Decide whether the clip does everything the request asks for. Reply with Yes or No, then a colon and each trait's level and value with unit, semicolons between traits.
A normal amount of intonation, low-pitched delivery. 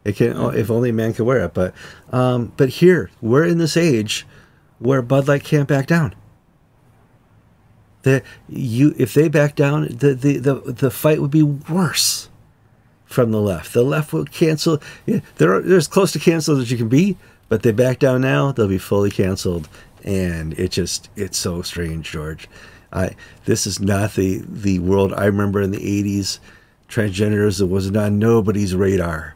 No: wide, 5.9 semitones; low, 115 Hz